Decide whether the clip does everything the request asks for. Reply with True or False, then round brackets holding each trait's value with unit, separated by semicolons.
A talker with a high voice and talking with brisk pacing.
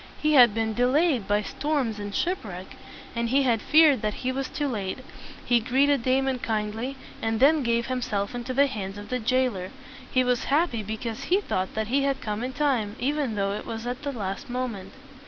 True (245 Hz; 210 wpm)